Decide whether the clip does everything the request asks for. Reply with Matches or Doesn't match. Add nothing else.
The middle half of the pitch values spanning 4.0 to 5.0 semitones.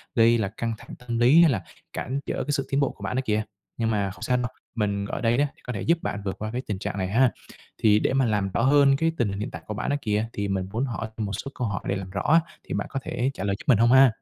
Matches